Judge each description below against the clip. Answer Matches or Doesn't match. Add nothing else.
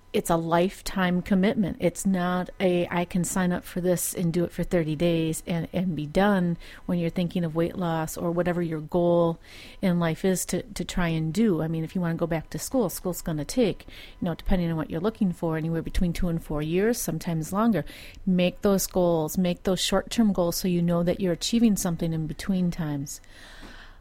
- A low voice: Doesn't match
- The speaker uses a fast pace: Matches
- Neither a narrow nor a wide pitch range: Doesn't match